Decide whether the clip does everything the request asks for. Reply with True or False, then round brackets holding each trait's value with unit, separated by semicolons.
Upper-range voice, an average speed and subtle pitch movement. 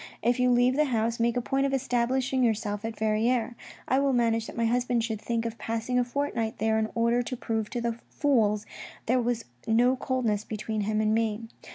False (235 Hz; 210 wpm; 2.0 semitones)